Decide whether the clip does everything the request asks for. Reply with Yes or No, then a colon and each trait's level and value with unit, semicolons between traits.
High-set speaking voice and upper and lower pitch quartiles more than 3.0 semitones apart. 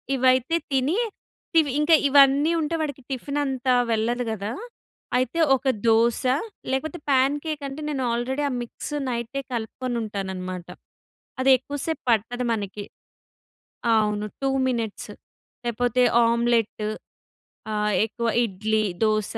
Yes: high, 245 Hz; average, 3.7 semitones